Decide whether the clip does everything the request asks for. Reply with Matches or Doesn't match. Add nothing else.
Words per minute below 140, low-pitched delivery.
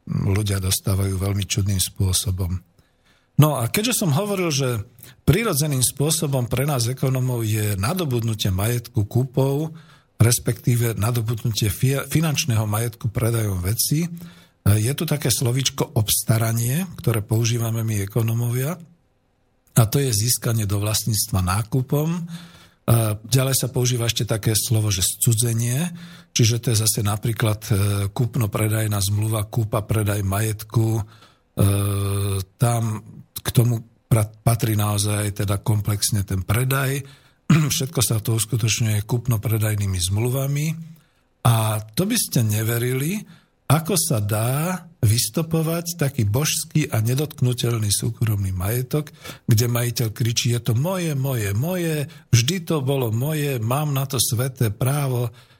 Matches